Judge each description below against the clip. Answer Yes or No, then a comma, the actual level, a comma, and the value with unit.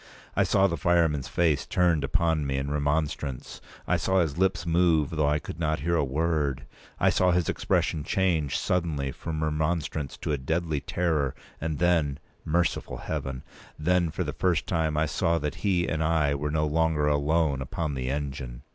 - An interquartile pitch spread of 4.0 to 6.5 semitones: No, average, 2.8 semitones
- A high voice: No, very low, 80 Hz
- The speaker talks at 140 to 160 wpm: No, average, 175 wpm